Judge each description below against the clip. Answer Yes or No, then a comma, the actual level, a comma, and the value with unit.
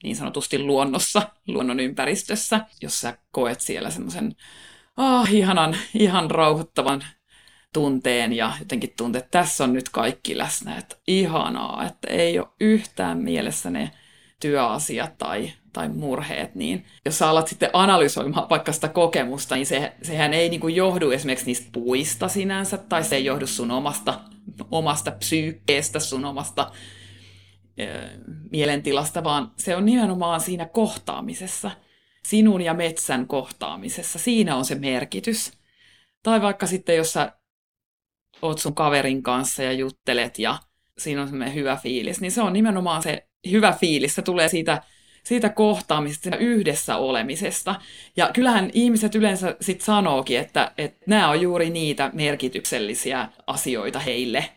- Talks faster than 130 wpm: Yes, average, 140 wpm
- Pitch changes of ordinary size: No, wide, 6.4 semitones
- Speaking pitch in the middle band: Yes, medium, 160 Hz